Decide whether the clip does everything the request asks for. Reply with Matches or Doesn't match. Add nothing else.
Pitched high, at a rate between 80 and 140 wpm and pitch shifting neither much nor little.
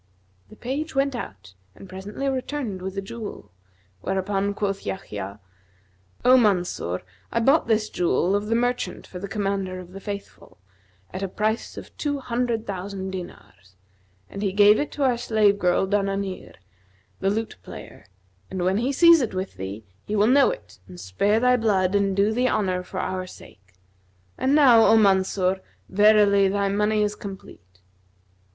Doesn't match